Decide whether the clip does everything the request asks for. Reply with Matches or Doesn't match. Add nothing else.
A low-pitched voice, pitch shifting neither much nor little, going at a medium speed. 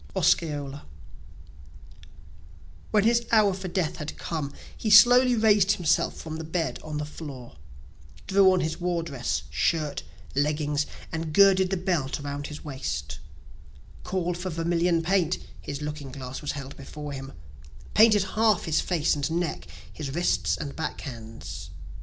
Doesn't match